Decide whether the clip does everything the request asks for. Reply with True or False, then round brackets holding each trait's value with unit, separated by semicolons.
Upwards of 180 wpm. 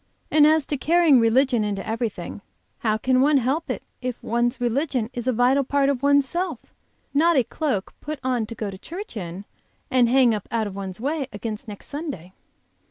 True (195 wpm)